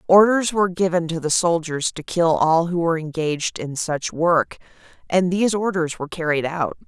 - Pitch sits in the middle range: Yes, medium, 170 Hz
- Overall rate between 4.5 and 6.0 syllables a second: Yes, 5.2 syllables/s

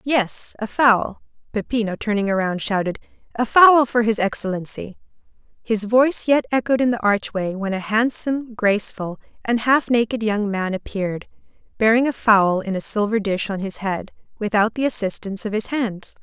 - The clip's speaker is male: No, female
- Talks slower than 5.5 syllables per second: Yes, 5.1 syllables/s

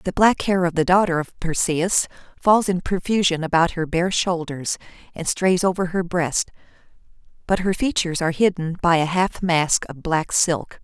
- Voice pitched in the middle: Yes, medium, 175 Hz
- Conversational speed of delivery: Yes, average, 175 wpm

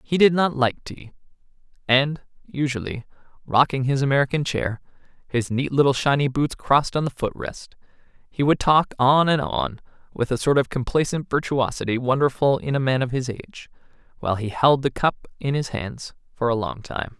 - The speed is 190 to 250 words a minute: No, average, 180 wpm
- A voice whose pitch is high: No, low, 135 Hz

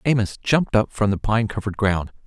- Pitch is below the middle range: Yes, low, 105 Hz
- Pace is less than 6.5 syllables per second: Yes, 6.0 syllables/s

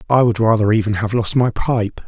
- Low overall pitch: Yes, low, 110 Hz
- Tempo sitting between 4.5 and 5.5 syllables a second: Yes, 5.4 syllables/s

